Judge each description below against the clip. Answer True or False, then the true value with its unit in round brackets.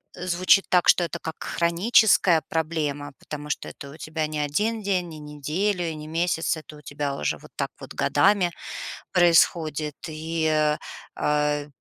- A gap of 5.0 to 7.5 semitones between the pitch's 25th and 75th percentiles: False (2.8 semitones)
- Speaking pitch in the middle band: True (160 Hz)